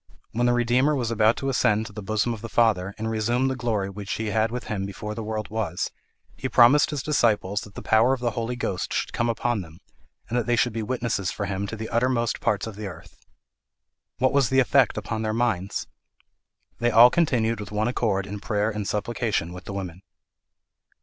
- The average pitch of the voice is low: Yes, low, 110 Hz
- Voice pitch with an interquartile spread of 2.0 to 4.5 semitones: Yes, average, 2.7 semitones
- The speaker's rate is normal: No, fast, 215 wpm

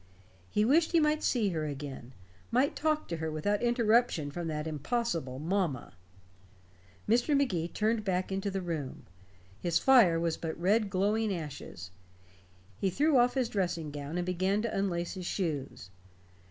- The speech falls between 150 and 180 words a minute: Yes, average, 155 wpm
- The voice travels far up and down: Yes, wide, 6.3 semitones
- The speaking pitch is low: No, medium, 185 Hz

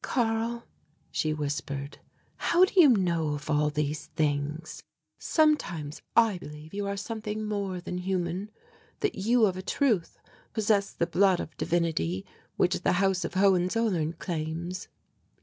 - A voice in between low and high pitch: Yes, medium, 180 Hz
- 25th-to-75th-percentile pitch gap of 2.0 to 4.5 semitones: No, average, 5.3 semitones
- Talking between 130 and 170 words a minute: Yes, average, 140 wpm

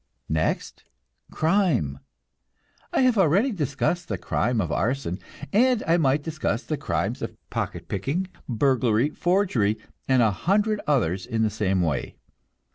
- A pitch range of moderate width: No, wide, 8.5 semitones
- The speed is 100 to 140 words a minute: Yes, slow, 135 wpm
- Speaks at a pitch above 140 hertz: No, low, 135 Hz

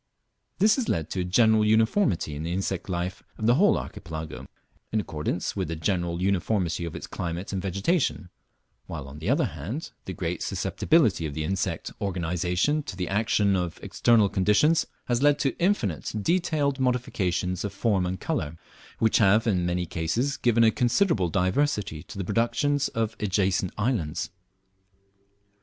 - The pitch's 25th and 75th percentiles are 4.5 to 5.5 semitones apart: Yes, average, 5.2 semitones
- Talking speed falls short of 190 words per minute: Yes, average, 160 wpm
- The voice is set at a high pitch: No, low, 100 Hz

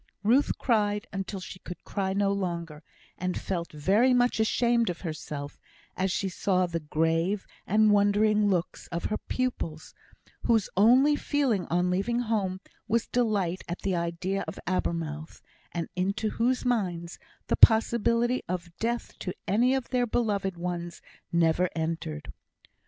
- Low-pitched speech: No, high, 195 Hz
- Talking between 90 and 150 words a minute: Yes, average, 145 wpm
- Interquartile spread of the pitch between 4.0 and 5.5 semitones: Yes, average, 4.6 semitones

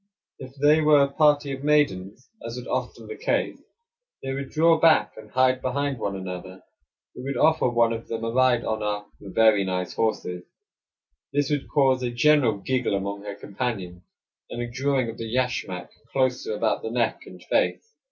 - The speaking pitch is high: No, low, 120 Hz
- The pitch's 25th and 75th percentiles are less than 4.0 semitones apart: No, average, 4.8 semitones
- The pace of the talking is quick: No, average, 180 wpm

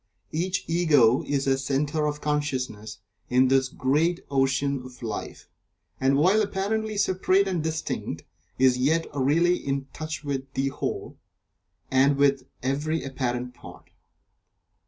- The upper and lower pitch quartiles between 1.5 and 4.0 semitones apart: Yes, average, 3.6 semitones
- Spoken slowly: Yes, slow, 130 wpm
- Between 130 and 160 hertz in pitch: Yes, medium, 140 Hz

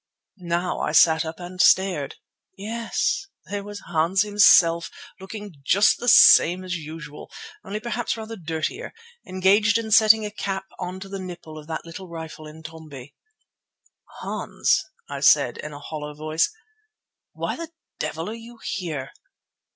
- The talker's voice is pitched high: No, medium, 180 Hz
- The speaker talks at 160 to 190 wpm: No, average, 145 wpm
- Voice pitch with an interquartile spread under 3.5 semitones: No, average, 4.5 semitones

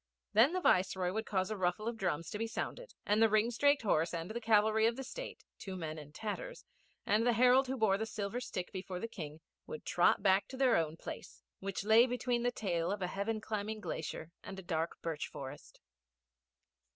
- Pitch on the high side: Yes, high, 210 Hz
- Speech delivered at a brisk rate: Yes, fast, 210 wpm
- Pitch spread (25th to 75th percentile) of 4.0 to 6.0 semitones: Yes, average, 4.3 semitones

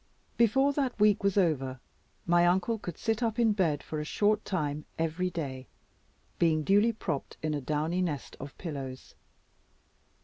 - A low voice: No, medium, 175 Hz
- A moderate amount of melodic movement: No, wide, 5.8 semitones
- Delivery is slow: No, average, 160 wpm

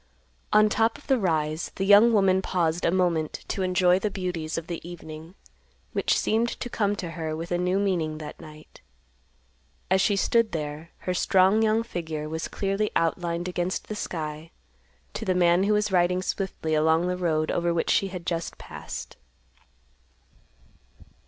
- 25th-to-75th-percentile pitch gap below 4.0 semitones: Yes, average, 3.3 semitones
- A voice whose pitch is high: No, medium, 180 Hz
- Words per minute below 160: No, average, 170 wpm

